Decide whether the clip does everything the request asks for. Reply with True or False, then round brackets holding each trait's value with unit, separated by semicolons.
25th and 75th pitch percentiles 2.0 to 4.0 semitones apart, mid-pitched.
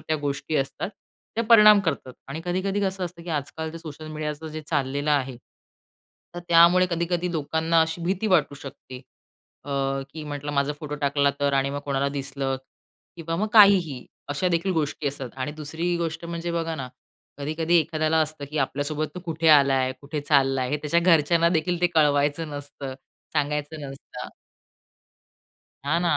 True (3.0 semitones; 155 Hz)